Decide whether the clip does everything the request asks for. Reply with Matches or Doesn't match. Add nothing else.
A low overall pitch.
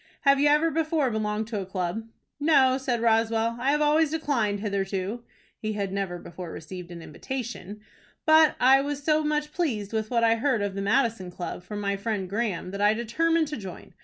Doesn't match